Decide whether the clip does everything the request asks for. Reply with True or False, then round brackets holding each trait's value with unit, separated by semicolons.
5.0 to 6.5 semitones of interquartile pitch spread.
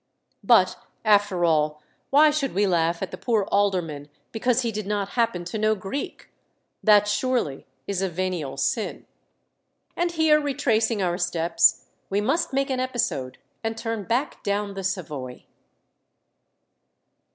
True (5.4 semitones)